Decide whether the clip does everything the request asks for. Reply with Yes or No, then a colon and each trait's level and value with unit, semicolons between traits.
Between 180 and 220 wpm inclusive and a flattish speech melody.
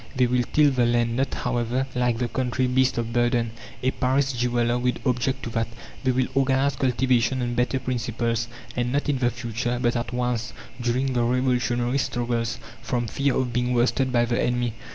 Yes: average, 190 wpm; narrow, 1.4 semitones